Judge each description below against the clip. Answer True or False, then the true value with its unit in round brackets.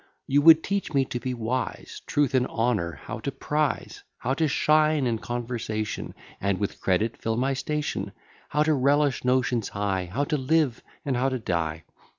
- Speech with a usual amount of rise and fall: True (4.6 semitones)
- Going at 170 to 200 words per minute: True (175 wpm)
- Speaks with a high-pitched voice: False (130 Hz)